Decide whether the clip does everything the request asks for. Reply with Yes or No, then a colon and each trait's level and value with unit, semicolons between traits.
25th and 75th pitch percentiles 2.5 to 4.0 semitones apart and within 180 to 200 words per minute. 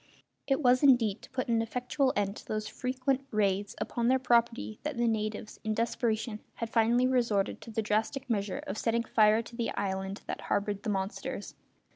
Yes: average, 2.8 semitones; average, 185 wpm